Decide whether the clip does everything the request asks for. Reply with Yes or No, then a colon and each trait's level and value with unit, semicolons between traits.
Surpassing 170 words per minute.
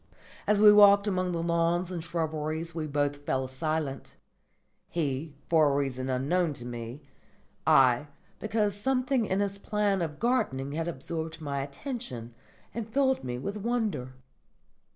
No: average, 145 wpm